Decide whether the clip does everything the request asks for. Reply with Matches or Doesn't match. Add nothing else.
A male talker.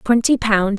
Doesn't match